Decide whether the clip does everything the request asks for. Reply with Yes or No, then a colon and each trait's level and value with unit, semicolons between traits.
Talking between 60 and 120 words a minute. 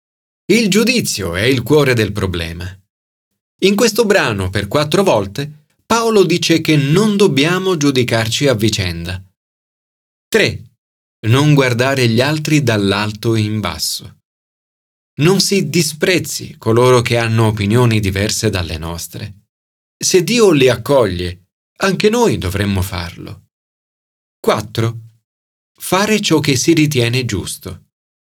Yes: slow, 115 wpm